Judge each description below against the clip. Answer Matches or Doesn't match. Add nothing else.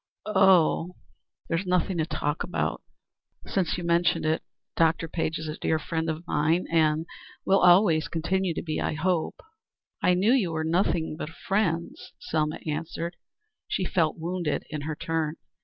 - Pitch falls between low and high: Matches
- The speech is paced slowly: Doesn't match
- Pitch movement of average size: Doesn't match